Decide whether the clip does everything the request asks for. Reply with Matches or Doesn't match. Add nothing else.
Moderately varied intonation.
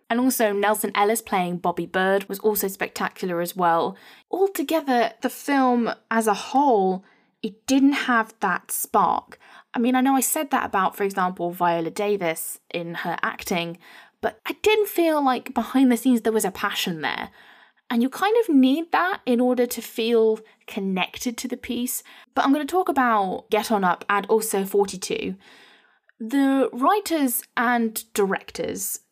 Matches